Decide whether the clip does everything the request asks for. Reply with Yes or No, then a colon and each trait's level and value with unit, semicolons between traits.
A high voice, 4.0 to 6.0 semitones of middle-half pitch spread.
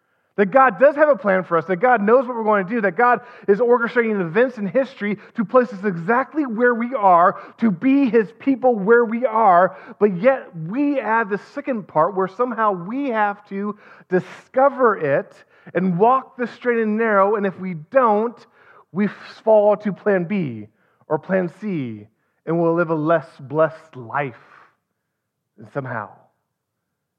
Yes: high, 210 Hz; average, 5.1 semitones